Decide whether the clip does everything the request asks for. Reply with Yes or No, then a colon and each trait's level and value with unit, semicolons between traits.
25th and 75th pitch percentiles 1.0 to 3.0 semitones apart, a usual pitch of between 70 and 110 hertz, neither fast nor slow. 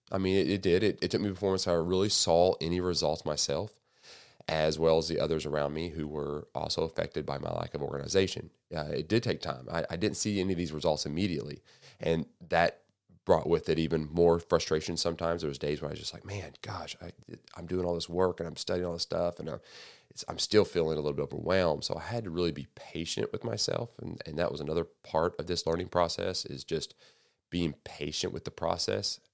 No: narrow, 2.5 semitones; very low, 85 Hz; fast, 230 wpm